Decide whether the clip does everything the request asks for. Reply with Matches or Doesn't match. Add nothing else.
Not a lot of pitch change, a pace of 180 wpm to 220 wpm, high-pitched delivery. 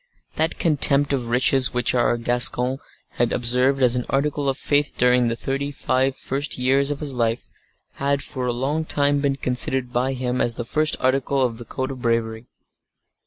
Doesn't match